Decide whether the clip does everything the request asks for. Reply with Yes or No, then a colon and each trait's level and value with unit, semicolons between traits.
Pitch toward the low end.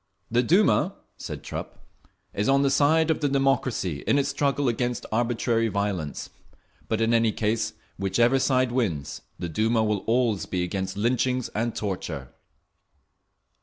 Yes: low, 115 Hz